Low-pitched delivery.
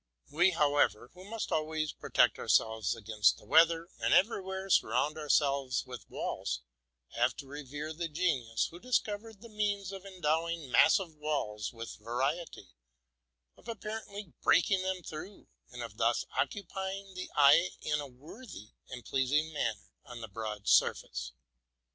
No: medium, 155 Hz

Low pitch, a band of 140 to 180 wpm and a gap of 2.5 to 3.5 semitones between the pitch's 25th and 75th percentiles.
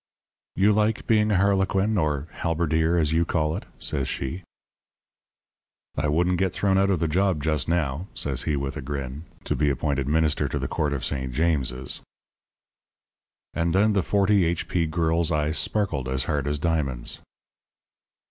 No: very low, 80 Hz; average, 165 wpm; average, 4.4 semitones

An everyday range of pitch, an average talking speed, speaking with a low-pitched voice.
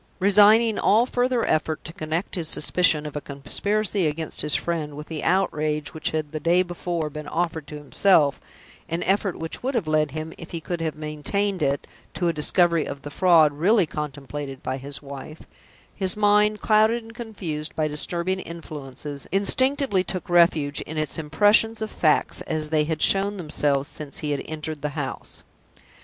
No: average, 4.4 semitones; average, 175 wpm; medium, 160 Hz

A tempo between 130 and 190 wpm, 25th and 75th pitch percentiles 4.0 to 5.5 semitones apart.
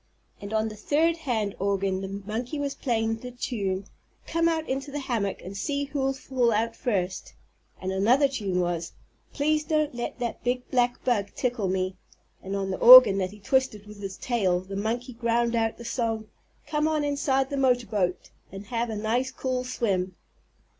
Yes: average, 180 wpm; average, 4.7 semitones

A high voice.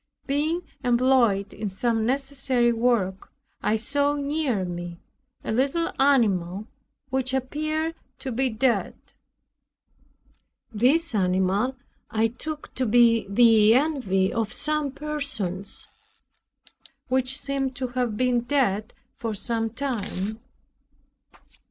Yes: high, 245 Hz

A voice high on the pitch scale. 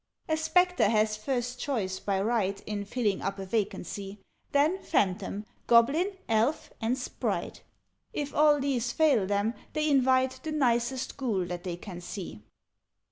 Yes: high, 235 Hz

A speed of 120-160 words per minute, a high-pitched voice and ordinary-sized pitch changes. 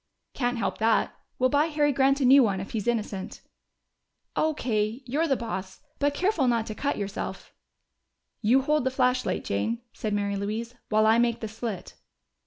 No: average, 175 wpm; high, 235 Hz; average, 4.1 semitones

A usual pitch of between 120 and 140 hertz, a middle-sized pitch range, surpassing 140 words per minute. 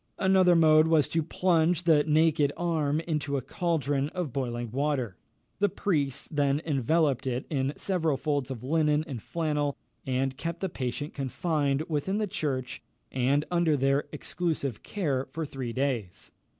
No: medium, 150 Hz; average, 3.3 semitones; average, 150 wpm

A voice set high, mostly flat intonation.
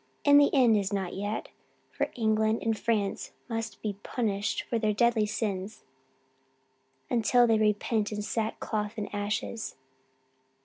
Yes: high, 215 Hz; narrow, 1.7 semitones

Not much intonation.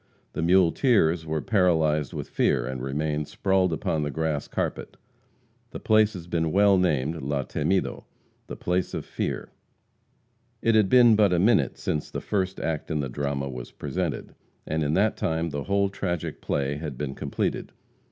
No: average, 4.6 semitones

